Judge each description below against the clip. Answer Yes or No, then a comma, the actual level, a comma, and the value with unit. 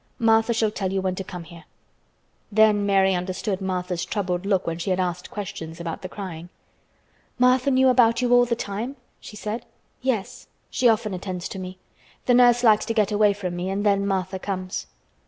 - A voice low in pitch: No, high, 200 Hz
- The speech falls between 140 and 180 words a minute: No, average, 195 wpm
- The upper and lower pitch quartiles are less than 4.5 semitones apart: Yes, average, 3.5 semitones